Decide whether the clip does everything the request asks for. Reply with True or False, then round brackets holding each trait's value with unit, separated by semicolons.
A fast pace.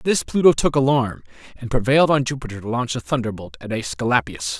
False (195 wpm)